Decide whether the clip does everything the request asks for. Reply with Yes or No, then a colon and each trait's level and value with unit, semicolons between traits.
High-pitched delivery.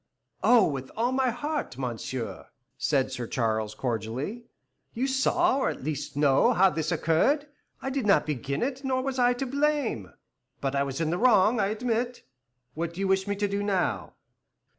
Yes: high, 195 Hz